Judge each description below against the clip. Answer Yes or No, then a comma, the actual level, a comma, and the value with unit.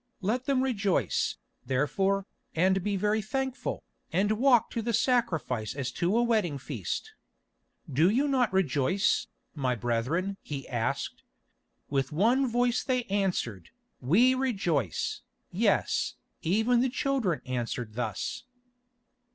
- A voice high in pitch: Yes, high, 195 Hz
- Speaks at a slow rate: Yes, slow, 120 wpm